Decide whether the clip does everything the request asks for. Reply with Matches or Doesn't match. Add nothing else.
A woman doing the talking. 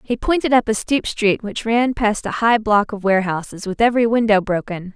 Matches